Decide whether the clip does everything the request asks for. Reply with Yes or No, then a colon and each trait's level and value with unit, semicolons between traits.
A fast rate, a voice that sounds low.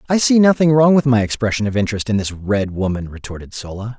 Yes: fast, 225 wpm; low, 115 Hz